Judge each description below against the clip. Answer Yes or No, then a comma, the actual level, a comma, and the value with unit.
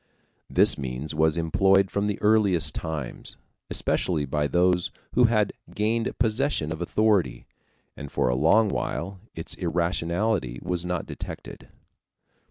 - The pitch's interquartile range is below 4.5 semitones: No, average, 5.1 semitones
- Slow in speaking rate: Yes, slow, 130 wpm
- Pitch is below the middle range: Yes, very low, 90 Hz